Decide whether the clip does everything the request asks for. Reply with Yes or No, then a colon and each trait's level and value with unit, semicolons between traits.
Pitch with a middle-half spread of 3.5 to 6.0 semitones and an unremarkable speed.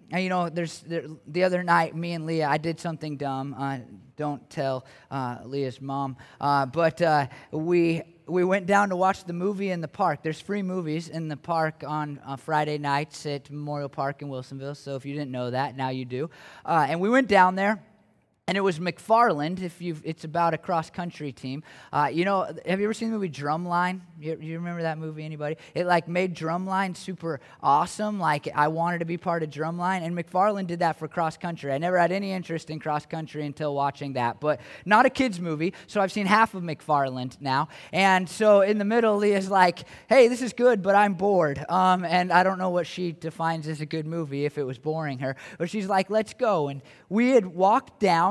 No: average, 3.9 semitones; fast, 220 wpm